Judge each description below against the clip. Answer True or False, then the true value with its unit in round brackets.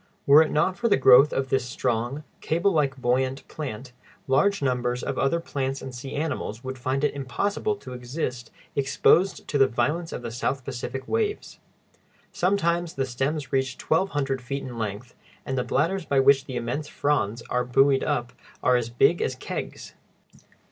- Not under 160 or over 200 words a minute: True (175 wpm)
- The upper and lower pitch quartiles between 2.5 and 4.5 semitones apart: True (3.5 semitones)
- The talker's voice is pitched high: False (135 Hz)